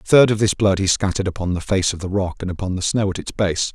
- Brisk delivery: Yes, fast, 320 wpm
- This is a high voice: No, very low, 95 Hz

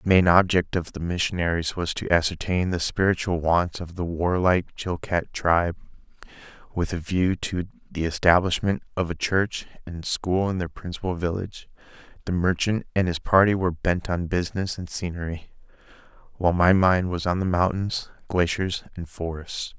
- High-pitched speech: No, very low, 90 Hz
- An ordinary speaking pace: Yes, average, 160 wpm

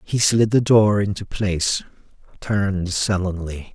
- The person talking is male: Yes, male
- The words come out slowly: Yes, slow, 130 wpm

